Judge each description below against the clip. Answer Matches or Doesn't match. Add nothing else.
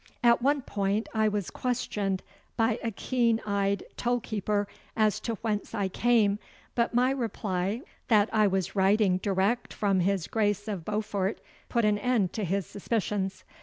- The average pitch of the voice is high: Matches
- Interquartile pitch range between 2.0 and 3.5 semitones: Matches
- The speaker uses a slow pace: Doesn't match